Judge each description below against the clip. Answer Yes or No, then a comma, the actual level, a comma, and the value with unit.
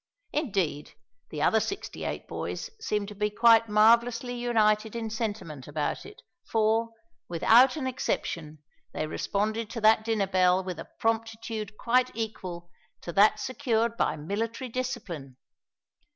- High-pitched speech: Yes, high, 220 Hz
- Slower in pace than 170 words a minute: Yes, slow, 135 wpm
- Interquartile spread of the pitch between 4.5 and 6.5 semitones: No, average, 3.8 semitones